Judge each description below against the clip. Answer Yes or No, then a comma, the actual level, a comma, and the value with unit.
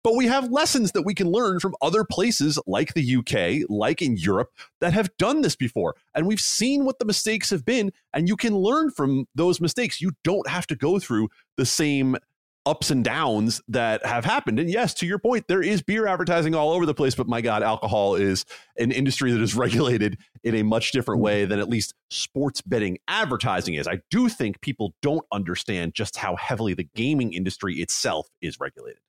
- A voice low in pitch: No, medium, 145 Hz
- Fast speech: Yes, fast, 210 wpm